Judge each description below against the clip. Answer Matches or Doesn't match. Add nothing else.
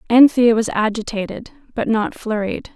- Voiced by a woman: Matches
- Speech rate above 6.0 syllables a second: Doesn't match